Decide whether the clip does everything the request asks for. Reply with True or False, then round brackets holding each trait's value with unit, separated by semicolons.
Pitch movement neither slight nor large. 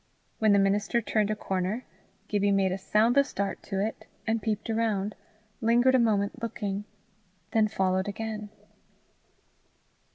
False (2.2 semitones)